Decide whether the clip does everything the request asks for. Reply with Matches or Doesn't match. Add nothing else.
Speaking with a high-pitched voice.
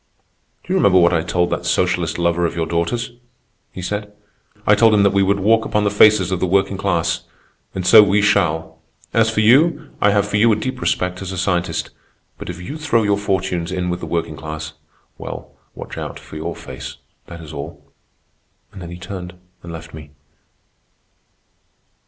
Doesn't match